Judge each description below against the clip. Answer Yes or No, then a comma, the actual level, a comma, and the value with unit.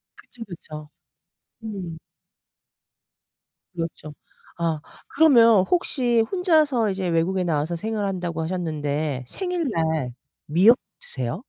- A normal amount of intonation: No, wide, 6.4 semitones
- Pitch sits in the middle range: Yes, medium, 180 Hz